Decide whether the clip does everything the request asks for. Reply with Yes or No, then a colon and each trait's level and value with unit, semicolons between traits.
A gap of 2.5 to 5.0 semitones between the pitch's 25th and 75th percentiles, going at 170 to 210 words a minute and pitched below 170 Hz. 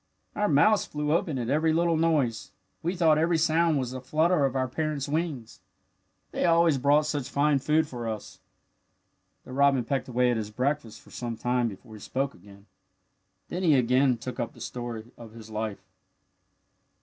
Yes: average, 4.7 semitones; average, 180 wpm; low, 135 Hz